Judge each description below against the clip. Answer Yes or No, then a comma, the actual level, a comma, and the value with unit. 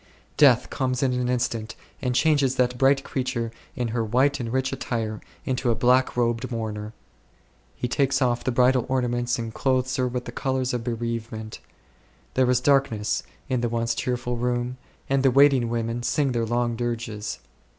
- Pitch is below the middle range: Yes, low, 125 Hz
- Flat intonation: Yes, narrow, 1.9 semitones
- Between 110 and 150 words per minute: No, average, 170 wpm